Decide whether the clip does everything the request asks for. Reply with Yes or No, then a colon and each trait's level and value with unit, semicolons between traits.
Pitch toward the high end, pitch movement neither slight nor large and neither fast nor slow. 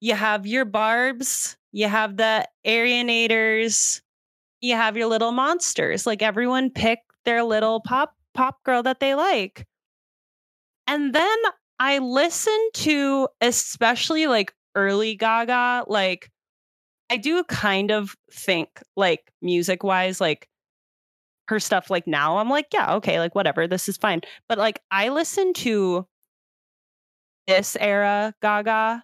No: high, 225 Hz; average, 4.1 semitones; slow, 130 wpm